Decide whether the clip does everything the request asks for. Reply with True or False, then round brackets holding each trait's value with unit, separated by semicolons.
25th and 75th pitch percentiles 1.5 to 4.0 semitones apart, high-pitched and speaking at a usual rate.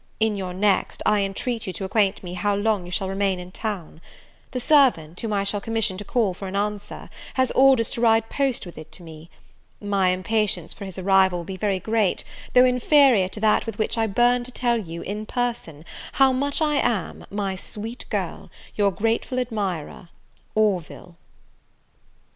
True (3.6 semitones; 205 Hz; 185 wpm)